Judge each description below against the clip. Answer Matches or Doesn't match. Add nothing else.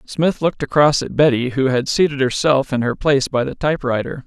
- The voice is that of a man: Matches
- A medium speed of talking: Doesn't match